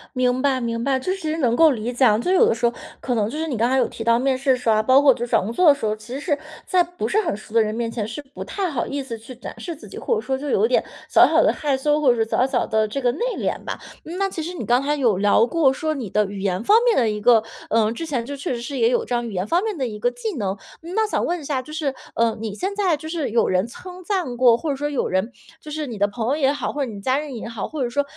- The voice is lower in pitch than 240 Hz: No, very high, 260 Hz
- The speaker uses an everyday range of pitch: Yes, average, 4.9 semitones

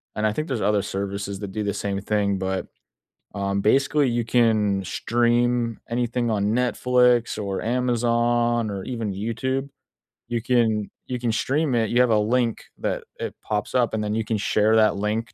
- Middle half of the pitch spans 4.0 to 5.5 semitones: No, average, 2.7 semitones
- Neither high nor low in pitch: No, low, 115 Hz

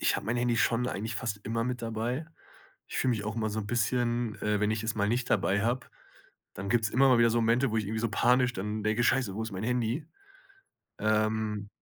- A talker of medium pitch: No, low, 115 Hz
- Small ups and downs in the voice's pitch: Yes, narrow, 2.1 semitones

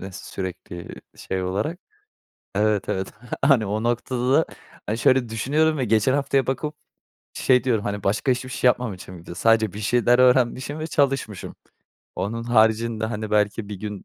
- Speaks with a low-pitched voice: Yes, low, 115 Hz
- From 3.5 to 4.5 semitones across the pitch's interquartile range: Yes, average, 3.8 semitones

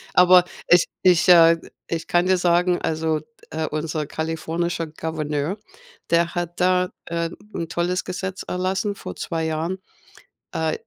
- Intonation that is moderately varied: No, narrow, 2.0 semitones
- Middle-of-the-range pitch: Yes, medium, 170 Hz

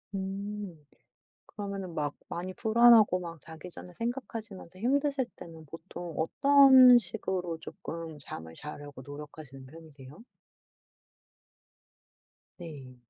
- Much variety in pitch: Yes, wide, 6.0 semitones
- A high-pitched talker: No, medium, 175 Hz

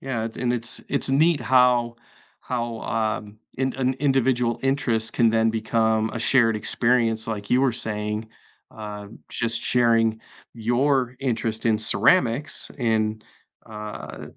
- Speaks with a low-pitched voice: Yes, low, 115 Hz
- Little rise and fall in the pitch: Yes, narrow, 2.2 semitones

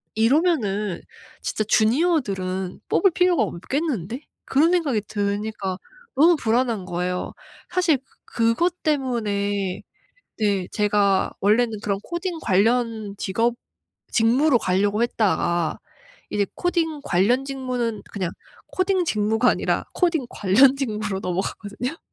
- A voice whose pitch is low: No, high, 225 Hz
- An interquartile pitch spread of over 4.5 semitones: Yes, wide, 5.5 semitones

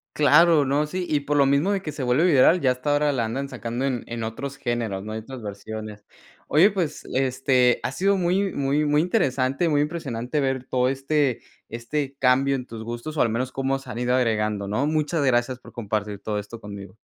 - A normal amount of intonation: Yes, average, 4.0 semitones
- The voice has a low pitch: Yes, low, 130 Hz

